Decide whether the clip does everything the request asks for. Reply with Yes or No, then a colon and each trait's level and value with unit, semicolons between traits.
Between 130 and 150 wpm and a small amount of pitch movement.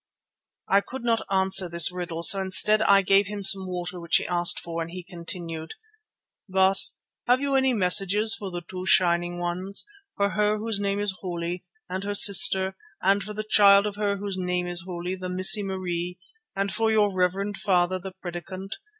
No: average, 185 wpm; narrow, 2.2 semitones